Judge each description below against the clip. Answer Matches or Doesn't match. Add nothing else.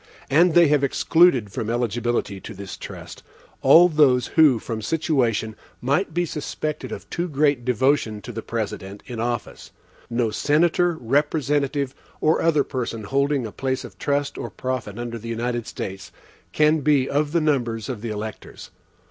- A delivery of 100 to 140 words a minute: Doesn't match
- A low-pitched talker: Matches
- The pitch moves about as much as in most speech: Matches